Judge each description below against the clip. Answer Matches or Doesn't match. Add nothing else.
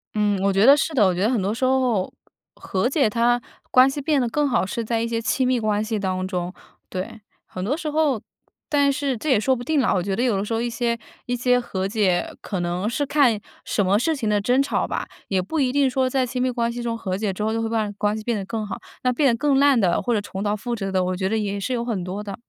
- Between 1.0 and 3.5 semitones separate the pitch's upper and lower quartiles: Doesn't match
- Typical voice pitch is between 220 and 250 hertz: Matches